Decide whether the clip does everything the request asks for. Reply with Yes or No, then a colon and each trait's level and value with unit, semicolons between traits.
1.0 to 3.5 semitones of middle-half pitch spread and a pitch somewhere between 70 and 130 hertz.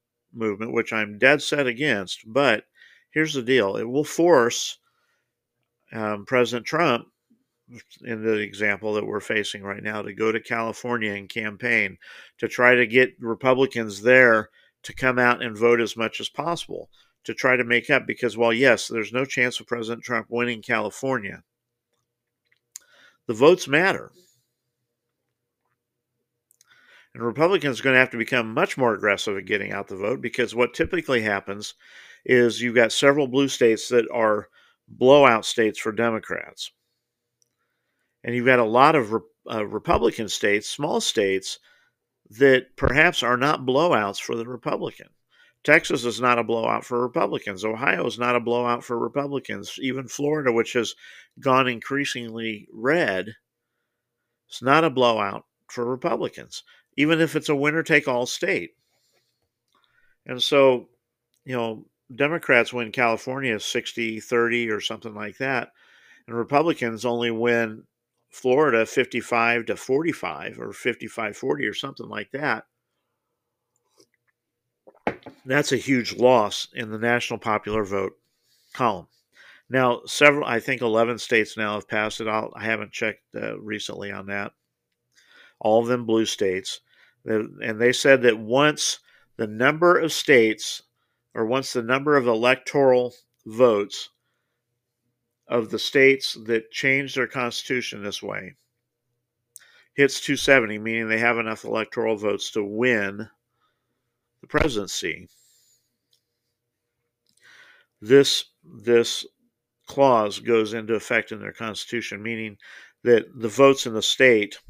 Yes: narrow, 2.4 semitones; low, 120 Hz